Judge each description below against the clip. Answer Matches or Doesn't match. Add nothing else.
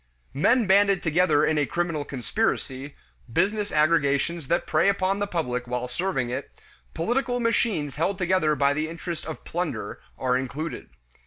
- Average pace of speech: Matches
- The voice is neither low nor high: Matches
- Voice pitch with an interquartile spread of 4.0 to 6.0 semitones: Matches